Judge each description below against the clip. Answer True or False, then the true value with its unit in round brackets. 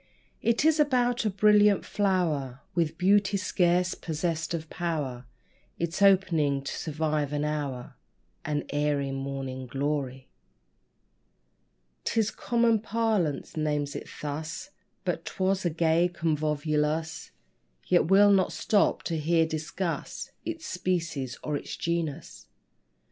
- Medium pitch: True (165 Hz)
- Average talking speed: False (115 wpm)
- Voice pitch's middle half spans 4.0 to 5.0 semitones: True (4.7 semitones)